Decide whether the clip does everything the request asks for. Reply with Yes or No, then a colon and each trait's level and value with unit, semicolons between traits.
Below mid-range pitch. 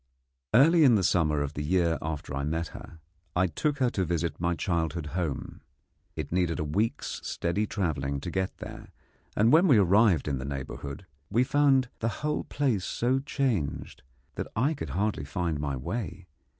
Yes: very low, 90 Hz